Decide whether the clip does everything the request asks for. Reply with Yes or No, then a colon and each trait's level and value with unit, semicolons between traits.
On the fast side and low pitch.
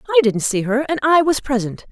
No: fast, 250 wpm; very high, 265 Hz